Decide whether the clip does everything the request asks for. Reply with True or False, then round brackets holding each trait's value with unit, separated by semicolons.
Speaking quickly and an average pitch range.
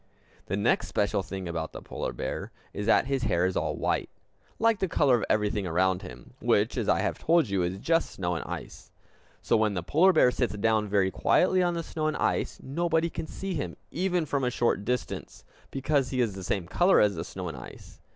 False (220 wpm; 8.9 semitones)